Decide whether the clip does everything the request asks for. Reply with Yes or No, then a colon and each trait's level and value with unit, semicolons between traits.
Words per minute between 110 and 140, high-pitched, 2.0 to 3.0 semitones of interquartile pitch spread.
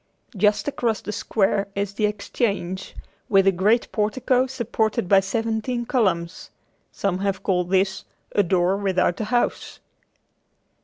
Yes: slow, 135 wpm; high, 200 Hz; average, 2.7 semitones